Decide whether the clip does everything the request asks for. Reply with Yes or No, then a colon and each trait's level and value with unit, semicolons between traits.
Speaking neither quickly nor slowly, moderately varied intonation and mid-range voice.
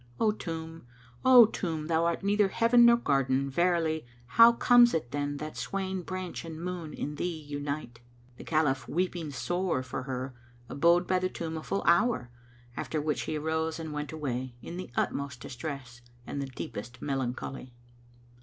Yes: average, 170 wpm; average, 4.7 semitones; medium, 160 Hz